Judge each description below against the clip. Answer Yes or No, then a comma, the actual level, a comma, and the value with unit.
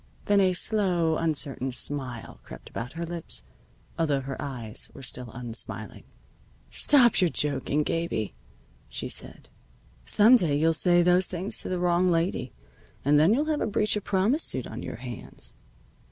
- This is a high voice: No, medium, 165 Hz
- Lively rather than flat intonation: Yes, wide, 6.0 semitones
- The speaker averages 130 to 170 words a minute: Yes, average, 160 wpm